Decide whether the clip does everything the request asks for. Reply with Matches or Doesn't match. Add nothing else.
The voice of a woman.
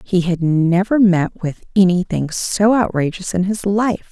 Matches